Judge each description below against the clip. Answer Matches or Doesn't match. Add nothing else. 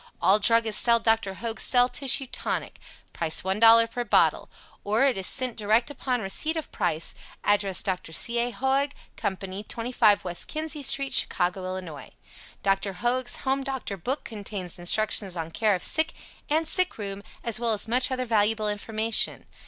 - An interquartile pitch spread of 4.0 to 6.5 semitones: Matches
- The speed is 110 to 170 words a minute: Matches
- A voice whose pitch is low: Doesn't match